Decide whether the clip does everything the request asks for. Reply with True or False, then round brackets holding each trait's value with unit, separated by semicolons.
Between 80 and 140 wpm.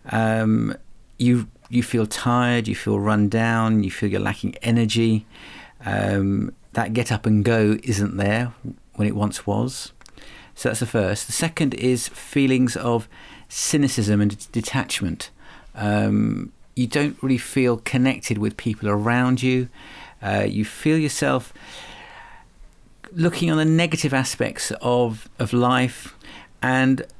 True (135 wpm)